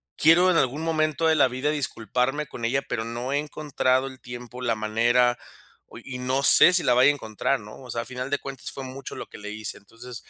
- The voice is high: No, low, 130 Hz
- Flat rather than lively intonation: No, average, 3.1 semitones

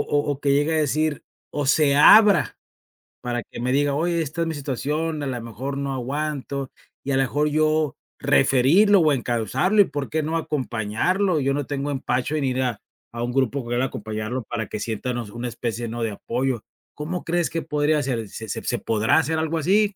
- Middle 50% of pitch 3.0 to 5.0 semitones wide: Yes, average, 4.0 semitones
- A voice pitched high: No, medium, 140 Hz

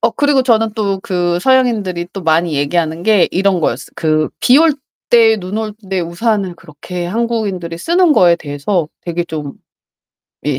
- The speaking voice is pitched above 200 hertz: No, medium, 185 Hz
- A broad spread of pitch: No, average, 4.8 semitones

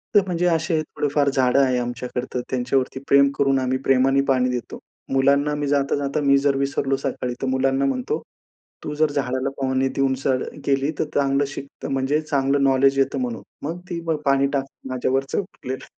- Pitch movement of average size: No, narrow, 1.3 semitones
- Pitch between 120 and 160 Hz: Yes, low, 135 Hz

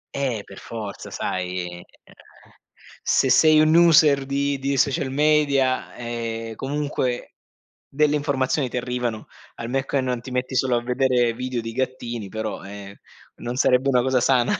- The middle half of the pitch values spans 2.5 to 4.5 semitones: Yes, average, 2.8 semitones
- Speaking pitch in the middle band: No, low, 125 Hz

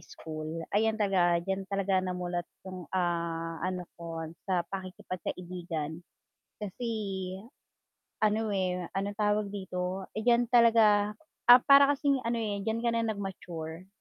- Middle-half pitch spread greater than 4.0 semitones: No, average, 3.4 semitones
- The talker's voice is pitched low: No, high, 190 Hz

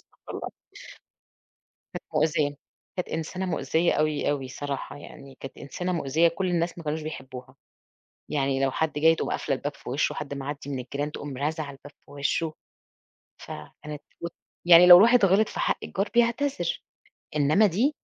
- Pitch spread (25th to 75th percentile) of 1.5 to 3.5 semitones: No, average, 3.9 semitones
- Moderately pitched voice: Yes, medium, 150 Hz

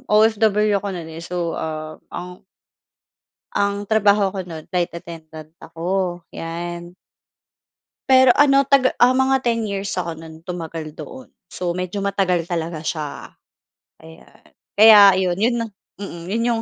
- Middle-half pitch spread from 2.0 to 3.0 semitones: No, average, 4.2 semitones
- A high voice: No, medium, 180 Hz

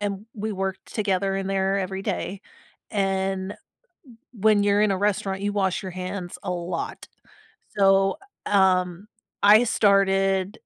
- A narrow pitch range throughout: Yes, narrow, 1.1 semitones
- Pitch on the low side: No, high, 195 Hz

